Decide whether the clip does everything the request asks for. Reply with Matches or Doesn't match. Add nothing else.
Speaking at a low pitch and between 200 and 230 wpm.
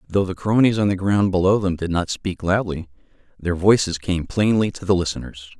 Matches